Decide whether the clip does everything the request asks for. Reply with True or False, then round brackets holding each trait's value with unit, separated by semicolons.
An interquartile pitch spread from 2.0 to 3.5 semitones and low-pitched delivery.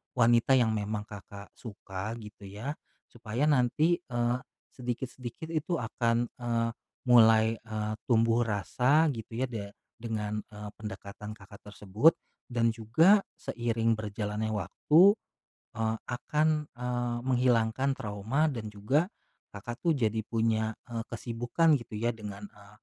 True (2.6 semitones; 115 Hz)